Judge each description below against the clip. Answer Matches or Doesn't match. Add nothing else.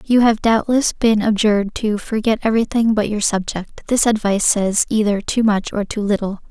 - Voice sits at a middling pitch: Doesn't match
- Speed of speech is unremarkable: Matches